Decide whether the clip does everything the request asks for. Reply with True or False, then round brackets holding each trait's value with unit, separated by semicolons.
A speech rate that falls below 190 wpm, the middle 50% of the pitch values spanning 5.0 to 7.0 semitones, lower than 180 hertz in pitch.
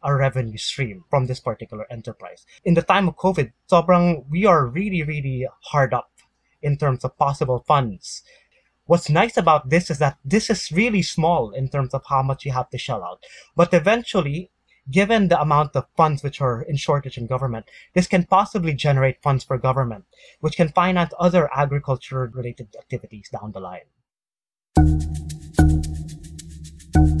True (160 wpm; 5.6 semitones; 140 Hz)